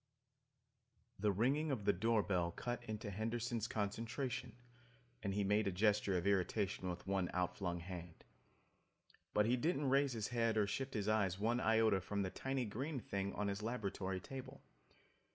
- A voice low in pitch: Yes, low, 105 Hz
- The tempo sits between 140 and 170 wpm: Yes, average, 165 wpm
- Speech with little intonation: No, average, 3.5 semitones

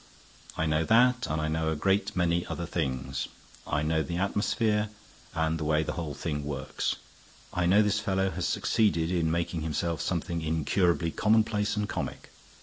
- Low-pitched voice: Yes, very low, 85 Hz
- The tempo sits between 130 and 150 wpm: No, average, 170 wpm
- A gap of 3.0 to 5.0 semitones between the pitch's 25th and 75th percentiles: Yes, average, 3.8 semitones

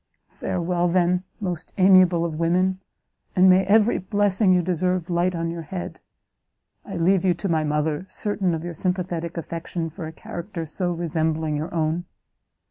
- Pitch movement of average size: No, narrow, 2.0 semitones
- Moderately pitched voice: Yes, medium, 175 Hz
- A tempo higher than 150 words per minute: Yes, average, 160 wpm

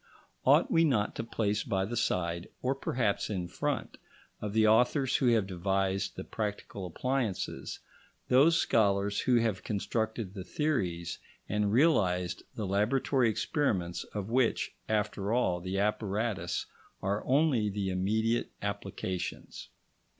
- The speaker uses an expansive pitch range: No, average, 3.8 semitones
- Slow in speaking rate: Yes, slow, 130 wpm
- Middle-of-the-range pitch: No, low, 105 Hz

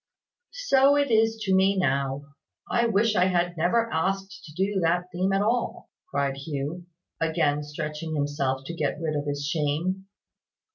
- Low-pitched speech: No, medium, 175 Hz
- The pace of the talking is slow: No, average, 160 wpm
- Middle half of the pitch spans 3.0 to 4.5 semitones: No, average, 5.0 semitones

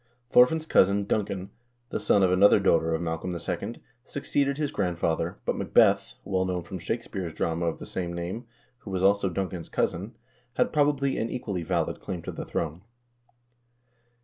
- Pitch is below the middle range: Yes, very low, 95 Hz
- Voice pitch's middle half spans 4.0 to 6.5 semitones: No, average, 3.5 semitones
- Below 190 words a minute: Yes, average, 170 wpm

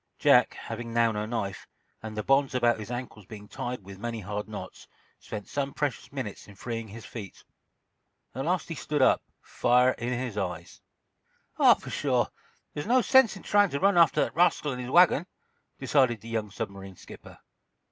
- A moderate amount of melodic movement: Yes, average, 4.9 semitones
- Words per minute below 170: No, average, 180 wpm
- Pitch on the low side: Yes, low, 120 Hz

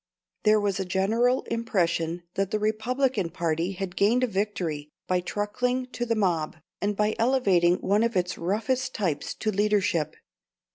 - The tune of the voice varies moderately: Yes, average, 4.1 semitones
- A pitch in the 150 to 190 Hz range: No, high, 205 Hz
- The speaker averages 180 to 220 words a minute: No, average, 155 wpm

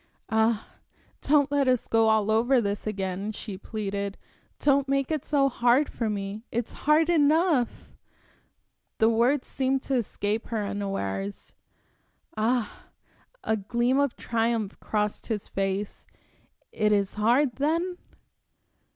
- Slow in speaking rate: Yes, slow, 125 wpm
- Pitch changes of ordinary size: Yes, average, 4.7 semitones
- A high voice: Yes, high, 230 Hz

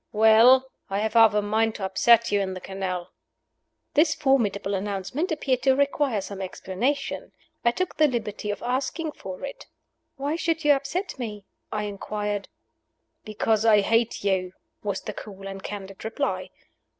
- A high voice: Yes, high, 220 Hz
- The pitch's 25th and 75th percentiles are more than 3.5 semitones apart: Yes, average, 5.2 semitones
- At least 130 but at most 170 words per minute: Yes, average, 160 wpm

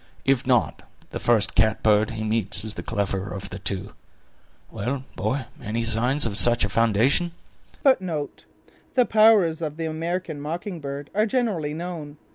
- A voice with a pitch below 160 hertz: Yes, medium, 140 Hz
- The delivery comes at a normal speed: Yes, average, 150 wpm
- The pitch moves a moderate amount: No, wide, 7.3 semitones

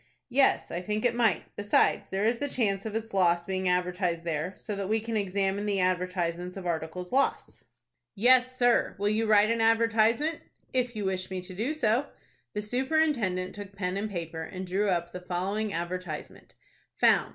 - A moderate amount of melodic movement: Yes, average, 3.9 semitones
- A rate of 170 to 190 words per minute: Yes, average, 185 wpm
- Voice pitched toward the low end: No, high, 200 Hz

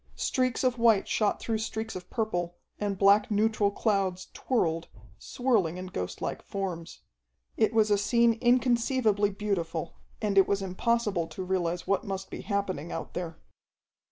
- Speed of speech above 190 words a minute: No, average, 150 wpm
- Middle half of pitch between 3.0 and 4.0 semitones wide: Yes, average, 3.4 semitones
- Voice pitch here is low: No, high, 200 Hz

